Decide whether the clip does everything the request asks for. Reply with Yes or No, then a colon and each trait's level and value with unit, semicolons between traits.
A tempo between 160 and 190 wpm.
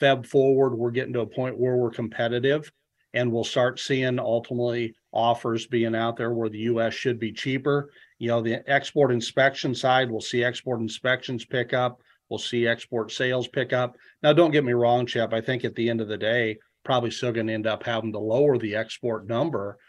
No: fast, 205 wpm